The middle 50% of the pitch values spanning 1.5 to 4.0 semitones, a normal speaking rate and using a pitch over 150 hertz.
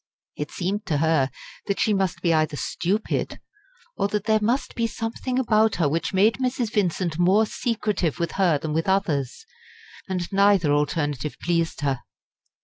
No: average, 5.0 semitones; average, 160 wpm; medium, 185 Hz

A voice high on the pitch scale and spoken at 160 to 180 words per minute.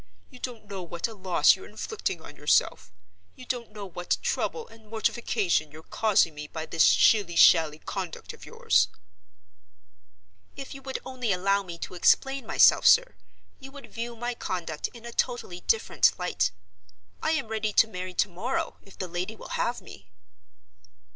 Yes: high, 210 Hz; average, 170 wpm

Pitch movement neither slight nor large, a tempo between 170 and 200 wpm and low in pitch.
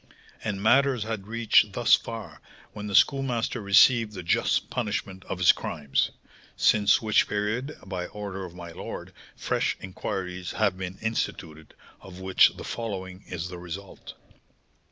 No: average, 3.5 semitones; average, 145 wpm; low, 100 Hz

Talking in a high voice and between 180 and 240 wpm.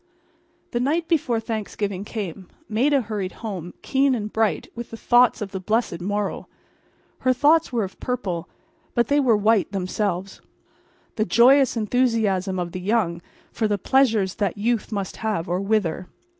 No: high, 215 Hz; average, 155 wpm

